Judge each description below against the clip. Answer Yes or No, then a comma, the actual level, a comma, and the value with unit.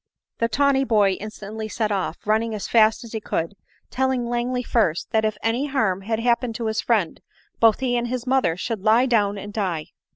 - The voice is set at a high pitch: Yes, high, 225 Hz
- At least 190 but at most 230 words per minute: Yes, average, 200 wpm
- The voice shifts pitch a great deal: No, average, 2.7 semitones